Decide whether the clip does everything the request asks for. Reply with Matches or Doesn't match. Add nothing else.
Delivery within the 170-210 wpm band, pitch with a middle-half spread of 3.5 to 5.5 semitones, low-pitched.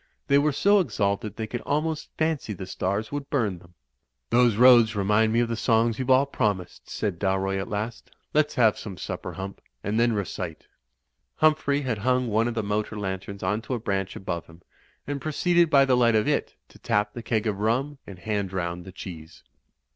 Matches